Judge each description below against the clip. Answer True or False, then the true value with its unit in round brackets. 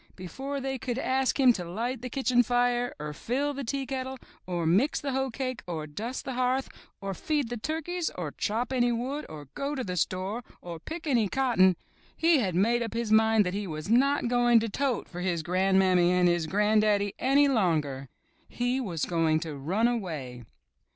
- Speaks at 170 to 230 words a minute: True (190 wpm)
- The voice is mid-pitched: False (230 Hz)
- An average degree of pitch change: False (6.5 semitones)